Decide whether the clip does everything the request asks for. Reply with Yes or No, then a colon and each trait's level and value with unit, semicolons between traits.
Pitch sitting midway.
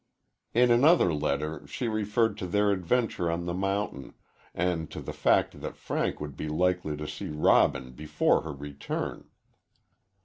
No: very low, 85 Hz